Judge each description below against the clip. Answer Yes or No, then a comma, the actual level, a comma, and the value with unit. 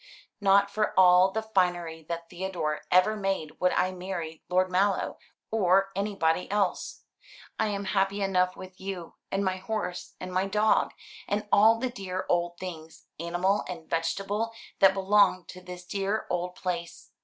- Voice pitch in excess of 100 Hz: Yes, medium, 185 Hz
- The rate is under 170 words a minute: Yes, average, 155 wpm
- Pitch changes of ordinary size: No, narrow, 1.9 semitones